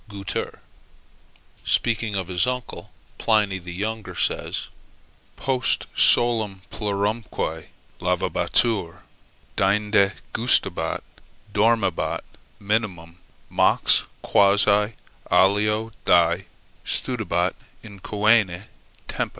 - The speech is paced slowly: Yes, slow, 75 wpm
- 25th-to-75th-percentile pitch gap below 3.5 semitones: Yes, average, 2.8 semitones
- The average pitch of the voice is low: Yes, low, 105 Hz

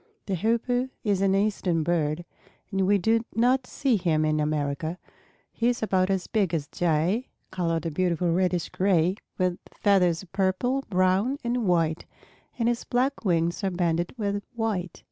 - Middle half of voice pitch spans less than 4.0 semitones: No, average, 4.5 semitones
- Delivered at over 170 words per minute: No, average, 165 wpm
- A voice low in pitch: No, medium, 185 Hz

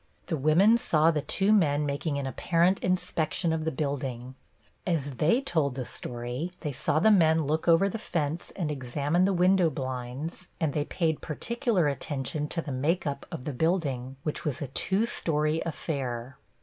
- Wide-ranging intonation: No, average, 3.7 semitones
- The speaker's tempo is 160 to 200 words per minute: Yes, average, 175 wpm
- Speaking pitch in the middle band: Yes, medium, 155 Hz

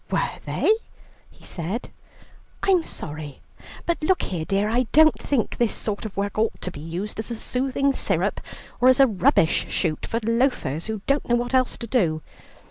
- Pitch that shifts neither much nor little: No, wide, 6.1 semitones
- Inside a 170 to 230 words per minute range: Yes, average, 185 wpm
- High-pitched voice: Yes, high, 225 Hz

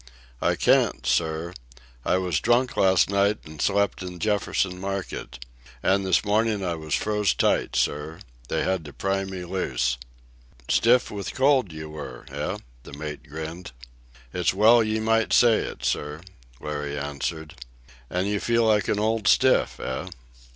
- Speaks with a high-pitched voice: No, very low, 95 Hz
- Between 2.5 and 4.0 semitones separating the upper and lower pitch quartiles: No, average, 5.2 semitones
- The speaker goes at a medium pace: Yes, average, 160 wpm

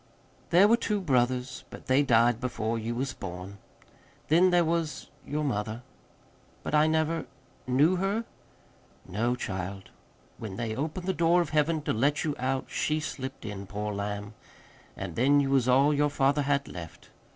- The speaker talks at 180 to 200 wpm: No, average, 165 wpm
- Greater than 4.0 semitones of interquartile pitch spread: Yes, wide, 5.6 semitones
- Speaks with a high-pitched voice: No, low, 135 Hz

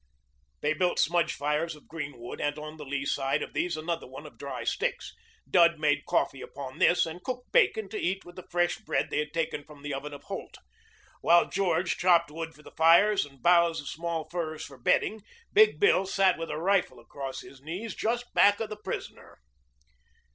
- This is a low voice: No, medium, 165 Hz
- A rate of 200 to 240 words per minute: Yes, fast, 205 wpm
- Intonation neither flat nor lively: Yes, average, 3.8 semitones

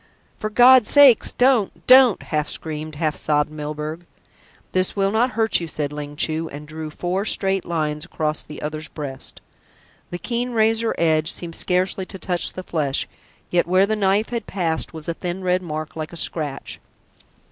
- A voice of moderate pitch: Yes, medium, 175 Hz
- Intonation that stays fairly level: No, average, 4.7 semitones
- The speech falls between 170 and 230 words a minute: Yes, average, 175 wpm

